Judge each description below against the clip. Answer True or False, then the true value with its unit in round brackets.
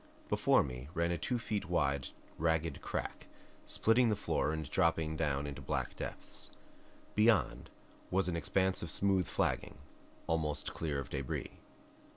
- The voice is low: True (80 Hz)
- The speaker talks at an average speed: True (145 wpm)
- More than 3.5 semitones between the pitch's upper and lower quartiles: True (4.5 semitones)